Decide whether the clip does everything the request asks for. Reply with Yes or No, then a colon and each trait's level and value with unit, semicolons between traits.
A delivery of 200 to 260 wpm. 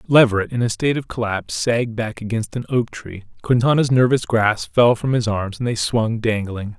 Yes: fast, 205 wpm